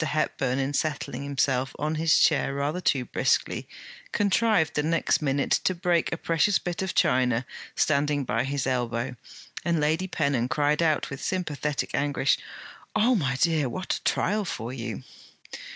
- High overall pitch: No, medium, 145 Hz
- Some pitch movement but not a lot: Yes, average, 3.9 semitones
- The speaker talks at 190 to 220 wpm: No, average, 155 wpm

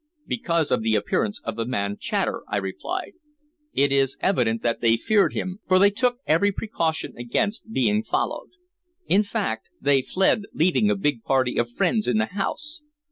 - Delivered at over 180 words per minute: No, average, 175 wpm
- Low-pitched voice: No, medium, 165 Hz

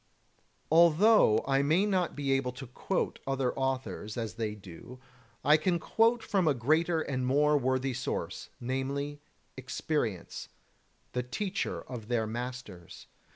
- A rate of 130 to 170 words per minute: Yes, average, 140 wpm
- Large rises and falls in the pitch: No, average, 4.0 semitones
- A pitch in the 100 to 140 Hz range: Yes, low, 135 Hz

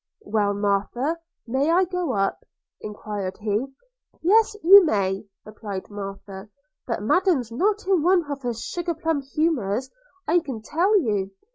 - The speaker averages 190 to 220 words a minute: No, average, 140 wpm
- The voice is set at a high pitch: Yes, very high, 255 Hz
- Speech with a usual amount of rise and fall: No, wide, 8.8 semitones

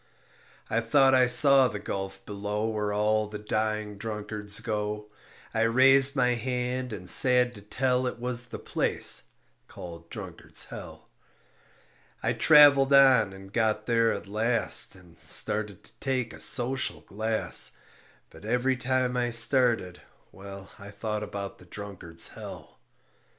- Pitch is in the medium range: No, low, 110 Hz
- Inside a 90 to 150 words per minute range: Yes, average, 140 wpm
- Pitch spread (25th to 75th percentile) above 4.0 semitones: No, average, 3.4 semitones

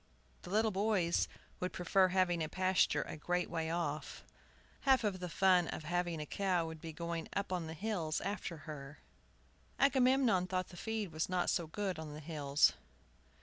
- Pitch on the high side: No, medium, 180 Hz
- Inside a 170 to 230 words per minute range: Yes, average, 175 wpm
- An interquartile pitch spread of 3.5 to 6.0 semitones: No, average, 3.1 semitones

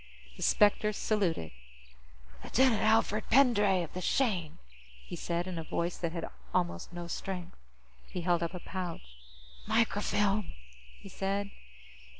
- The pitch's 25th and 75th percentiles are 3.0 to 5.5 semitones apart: Yes, average, 3.4 semitones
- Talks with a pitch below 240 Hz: Yes, medium, 185 Hz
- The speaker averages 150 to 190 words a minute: No, slow, 135 wpm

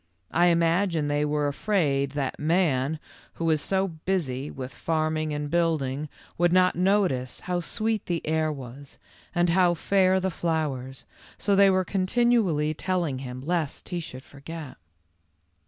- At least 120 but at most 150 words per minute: Yes, average, 145 wpm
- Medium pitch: Yes, medium, 160 Hz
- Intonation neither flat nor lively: Yes, average, 4.1 semitones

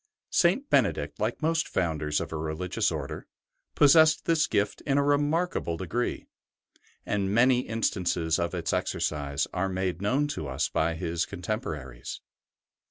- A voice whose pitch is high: No, very low, 95 Hz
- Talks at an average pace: Yes, average, 145 wpm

